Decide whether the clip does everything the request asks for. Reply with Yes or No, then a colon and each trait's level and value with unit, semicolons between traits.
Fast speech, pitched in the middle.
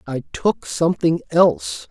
No: slow, 125 wpm; medium, 155 Hz